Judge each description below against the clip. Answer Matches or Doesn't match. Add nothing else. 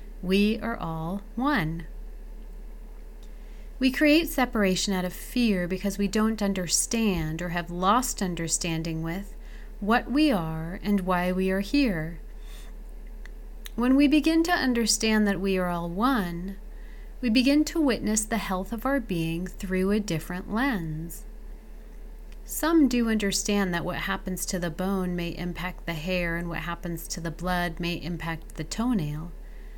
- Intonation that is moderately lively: Matches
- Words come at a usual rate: Matches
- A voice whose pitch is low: Doesn't match